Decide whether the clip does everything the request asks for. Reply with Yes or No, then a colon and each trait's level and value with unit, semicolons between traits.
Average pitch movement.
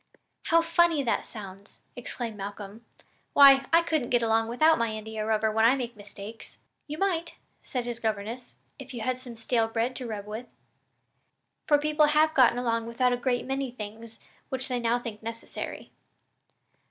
Yes: average, 3.4 semitones